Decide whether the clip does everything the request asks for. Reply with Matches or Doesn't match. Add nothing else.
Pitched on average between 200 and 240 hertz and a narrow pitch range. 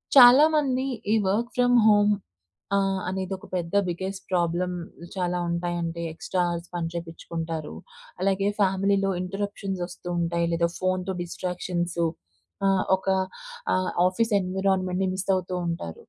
Doesn't match